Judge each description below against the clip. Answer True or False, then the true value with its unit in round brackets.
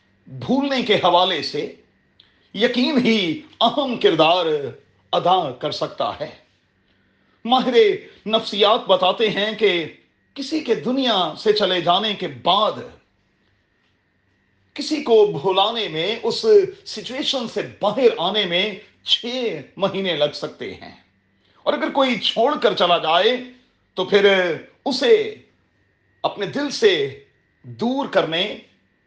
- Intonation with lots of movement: True (7.1 semitones)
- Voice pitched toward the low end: False (225 Hz)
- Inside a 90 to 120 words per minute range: True (115 wpm)